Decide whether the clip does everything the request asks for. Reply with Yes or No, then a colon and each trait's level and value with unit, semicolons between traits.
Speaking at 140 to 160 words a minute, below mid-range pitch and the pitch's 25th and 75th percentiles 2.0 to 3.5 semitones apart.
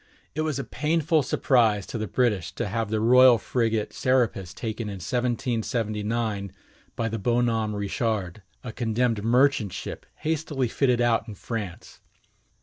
Yes: average, 150 wpm; low, 115 Hz; average, 2.9 semitones